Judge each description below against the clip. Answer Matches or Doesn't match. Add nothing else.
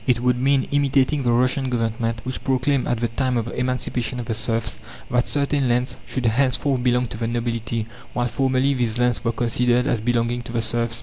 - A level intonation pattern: Matches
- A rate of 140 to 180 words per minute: Doesn't match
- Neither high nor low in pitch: Doesn't match